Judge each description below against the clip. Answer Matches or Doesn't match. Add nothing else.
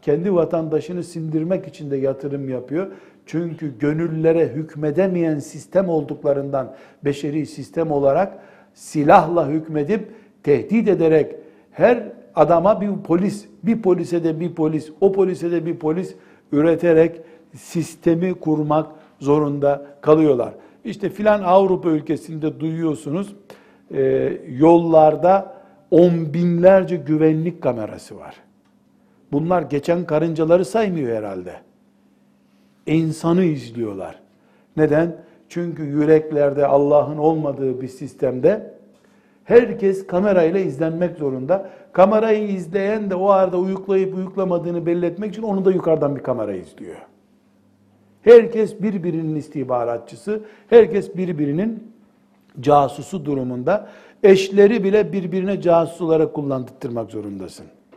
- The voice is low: Doesn't match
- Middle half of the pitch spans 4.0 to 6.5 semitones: Matches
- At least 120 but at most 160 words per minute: Doesn't match